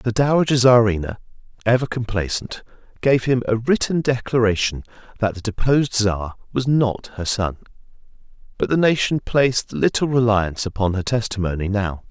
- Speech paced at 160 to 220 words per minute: No, average, 140 wpm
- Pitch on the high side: No, low, 115 Hz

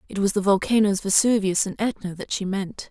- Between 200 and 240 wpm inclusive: Yes, fast, 205 wpm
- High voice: Yes, high, 200 Hz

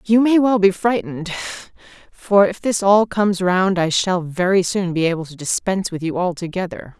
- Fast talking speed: No, average, 180 wpm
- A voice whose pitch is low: No, high, 190 Hz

